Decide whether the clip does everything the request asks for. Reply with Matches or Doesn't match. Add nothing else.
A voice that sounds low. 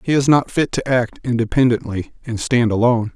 Matches